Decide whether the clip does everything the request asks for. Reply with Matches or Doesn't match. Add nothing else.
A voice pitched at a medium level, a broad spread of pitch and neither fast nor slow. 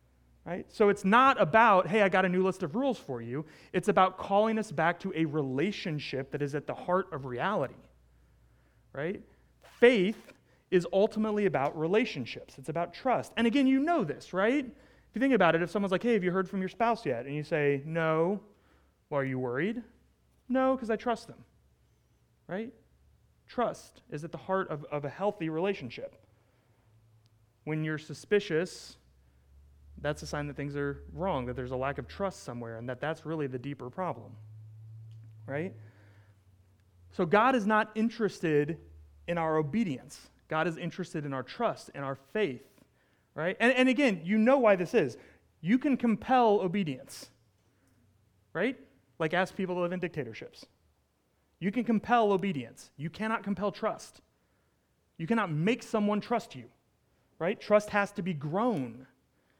Matches